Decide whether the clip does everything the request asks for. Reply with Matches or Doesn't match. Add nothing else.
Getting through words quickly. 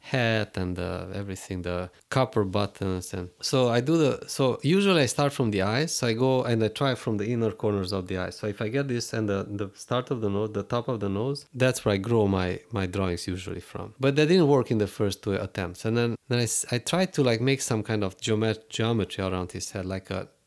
Matches